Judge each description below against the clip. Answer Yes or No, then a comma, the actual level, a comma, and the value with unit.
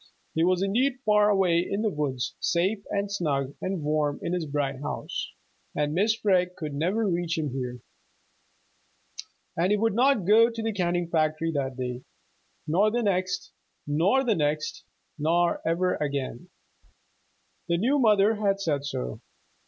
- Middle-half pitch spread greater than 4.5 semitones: Yes, wide, 5.4 semitones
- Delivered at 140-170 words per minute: Yes, average, 155 wpm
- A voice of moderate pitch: Yes, medium, 175 Hz